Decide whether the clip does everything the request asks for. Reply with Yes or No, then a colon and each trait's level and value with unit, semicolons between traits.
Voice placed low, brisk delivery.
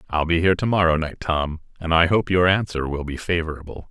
Yes: very low, 85 Hz; fast, 230 wpm